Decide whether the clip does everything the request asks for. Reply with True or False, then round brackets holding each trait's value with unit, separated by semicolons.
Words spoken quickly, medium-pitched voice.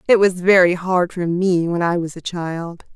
True (225 wpm; 175 Hz)